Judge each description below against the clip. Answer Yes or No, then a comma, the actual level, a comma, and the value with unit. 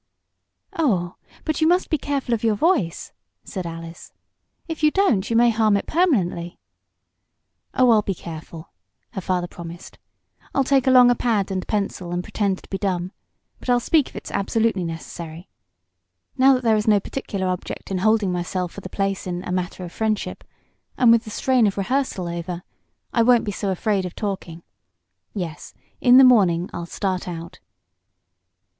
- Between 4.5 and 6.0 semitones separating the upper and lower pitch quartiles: Yes, average, 5.2 semitones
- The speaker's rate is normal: Yes, average, 175 wpm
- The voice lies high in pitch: Yes, high, 200 Hz